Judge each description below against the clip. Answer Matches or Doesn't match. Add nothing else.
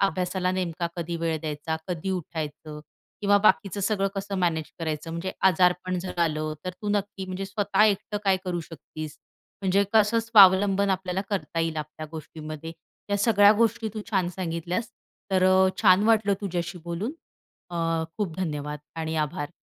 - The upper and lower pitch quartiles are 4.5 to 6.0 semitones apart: Doesn't match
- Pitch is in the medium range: Matches